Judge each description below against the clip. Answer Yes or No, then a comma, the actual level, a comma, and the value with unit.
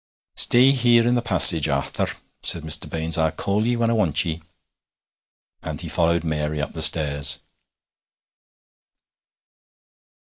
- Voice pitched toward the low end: Yes, very low, 85 Hz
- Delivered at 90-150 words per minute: Yes, slow, 135 wpm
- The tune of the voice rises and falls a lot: Yes, wide, 7.1 semitones